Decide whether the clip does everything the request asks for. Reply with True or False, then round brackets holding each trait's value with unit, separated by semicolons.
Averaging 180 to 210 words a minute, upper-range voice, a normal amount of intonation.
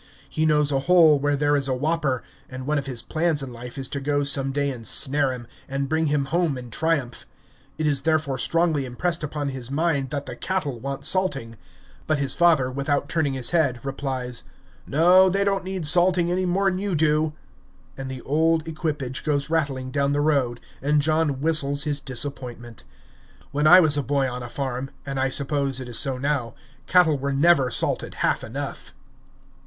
False (195 wpm; 145 Hz; 3.0 semitones)